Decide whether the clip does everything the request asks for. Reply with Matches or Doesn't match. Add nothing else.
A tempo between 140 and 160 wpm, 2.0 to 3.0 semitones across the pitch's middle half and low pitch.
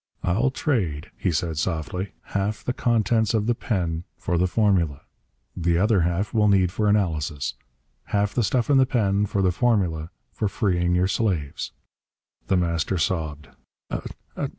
Doesn't match